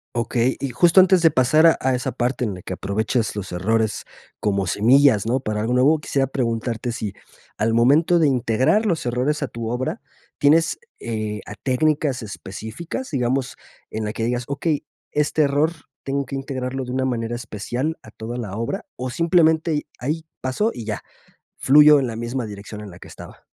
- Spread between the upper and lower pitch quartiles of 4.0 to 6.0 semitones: Yes, average, 4.6 semitones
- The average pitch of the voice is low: Yes, low, 125 Hz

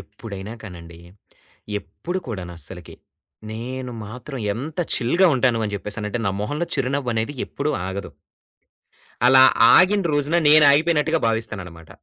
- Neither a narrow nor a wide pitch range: No, wide, 6.2 semitones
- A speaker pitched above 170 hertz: No, low, 120 Hz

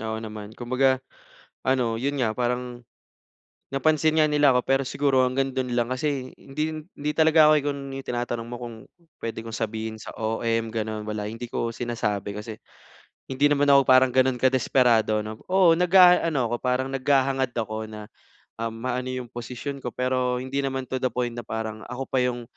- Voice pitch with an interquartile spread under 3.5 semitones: Yes, average, 2.9 semitones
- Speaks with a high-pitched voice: No, low, 125 Hz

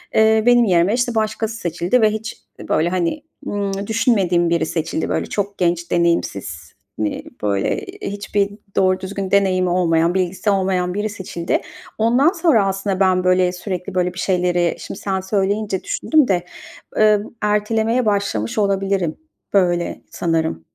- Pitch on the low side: No, high, 190 Hz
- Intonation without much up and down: No, average, 3.2 semitones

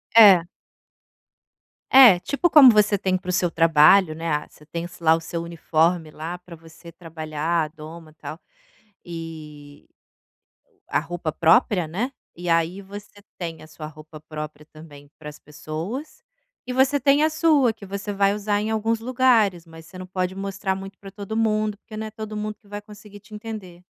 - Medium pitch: Yes, medium, 180 Hz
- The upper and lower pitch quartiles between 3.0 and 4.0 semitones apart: No, average, 4.6 semitones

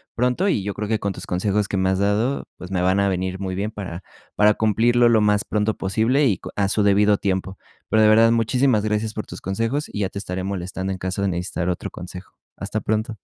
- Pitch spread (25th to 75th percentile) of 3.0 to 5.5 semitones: No, narrow, 2.6 semitones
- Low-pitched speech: Yes, low, 100 Hz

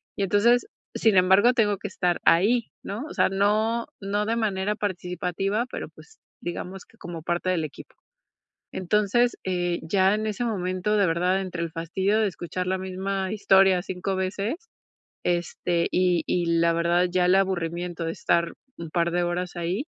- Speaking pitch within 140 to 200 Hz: Yes, high, 190 Hz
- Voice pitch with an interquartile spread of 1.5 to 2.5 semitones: No, average, 2.9 semitones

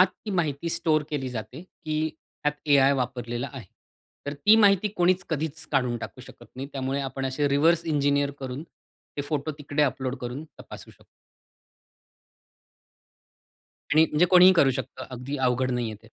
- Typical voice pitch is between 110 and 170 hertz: Yes, medium, 140 Hz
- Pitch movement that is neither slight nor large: Yes, average, 3.3 semitones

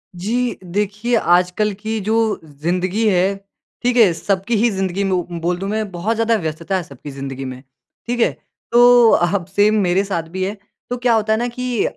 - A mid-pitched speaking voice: No, high, 200 Hz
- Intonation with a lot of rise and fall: No, average, 4.2 semitones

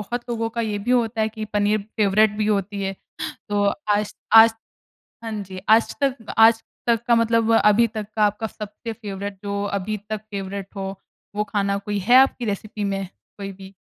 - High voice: Yes, high, 210 Hz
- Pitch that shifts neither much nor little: No, narrow, 2.1 semitones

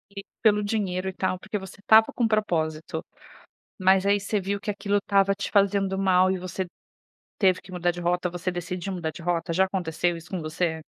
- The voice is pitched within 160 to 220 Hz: Yes, medium, 185 Hz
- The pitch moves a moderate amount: No, narrow, 2.2 semitones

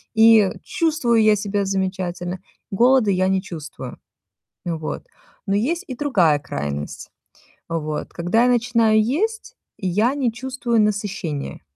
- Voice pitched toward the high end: Yes, high, 210 Hz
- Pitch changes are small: No, average, 5.3 semitones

